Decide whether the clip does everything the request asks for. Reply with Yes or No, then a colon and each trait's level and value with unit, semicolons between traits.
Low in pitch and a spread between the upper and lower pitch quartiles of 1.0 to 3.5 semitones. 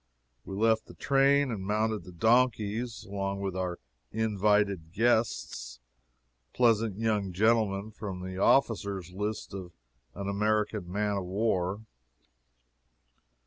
Yes: low, 105 Hz; narrow, 2.5 semitones